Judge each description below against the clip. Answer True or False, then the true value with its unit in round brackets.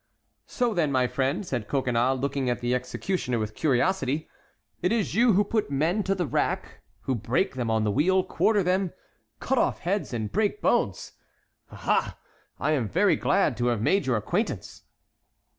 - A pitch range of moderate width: False (7.7 semitones)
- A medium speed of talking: True (175 wpm)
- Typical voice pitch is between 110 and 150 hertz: True (140 Hz)